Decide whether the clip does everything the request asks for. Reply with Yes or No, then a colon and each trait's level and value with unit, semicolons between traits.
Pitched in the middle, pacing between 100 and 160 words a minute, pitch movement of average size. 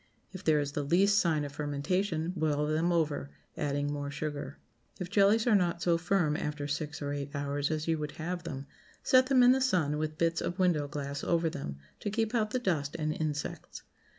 No: medium, 155 Hz; fast, 205 wpm; average, 3.9 semitones